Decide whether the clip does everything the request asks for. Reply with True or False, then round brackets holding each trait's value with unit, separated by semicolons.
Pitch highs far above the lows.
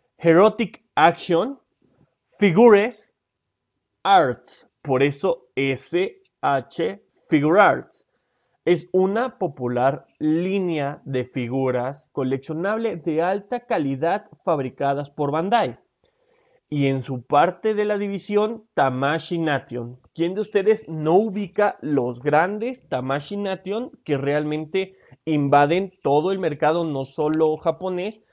True (6.4 semitones)